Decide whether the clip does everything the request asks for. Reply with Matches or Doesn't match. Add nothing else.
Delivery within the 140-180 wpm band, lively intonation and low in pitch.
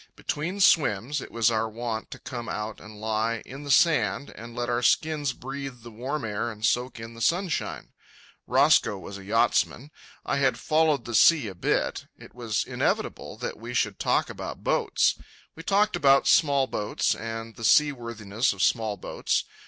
Doesn't match